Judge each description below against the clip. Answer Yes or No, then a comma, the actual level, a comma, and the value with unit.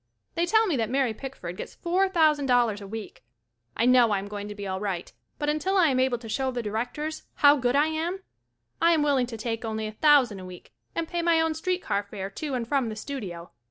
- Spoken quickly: Yes, fast, 240 wpm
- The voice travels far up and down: Yes, wide, 6.5 semitones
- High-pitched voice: Yes, very high, 255 Hz